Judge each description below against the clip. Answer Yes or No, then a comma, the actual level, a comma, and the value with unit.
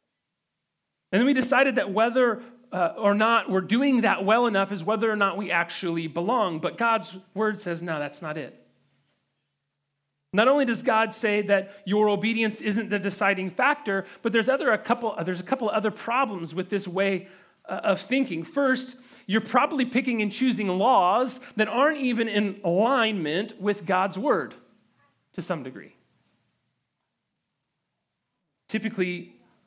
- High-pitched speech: Yes, high, 210 Hz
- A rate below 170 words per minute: Yes, average, 160 wpm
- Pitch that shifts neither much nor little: Yes, average, 4.1 semitones